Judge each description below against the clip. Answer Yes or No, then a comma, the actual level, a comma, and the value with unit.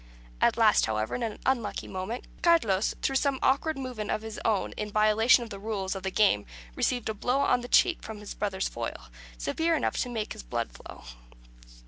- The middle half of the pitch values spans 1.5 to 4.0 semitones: No, average, 4.4 semitones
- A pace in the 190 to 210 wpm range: Yes, average, 200 wpm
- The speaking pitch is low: No, high, 220 Hz